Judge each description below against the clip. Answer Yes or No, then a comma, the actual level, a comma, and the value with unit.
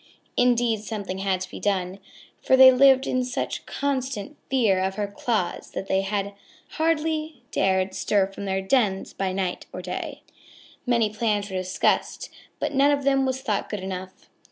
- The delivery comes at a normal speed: Yes, average, 165 wpm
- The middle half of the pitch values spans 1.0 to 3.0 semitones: No, wide, 5.4 semitones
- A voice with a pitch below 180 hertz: No, high, 210 Hz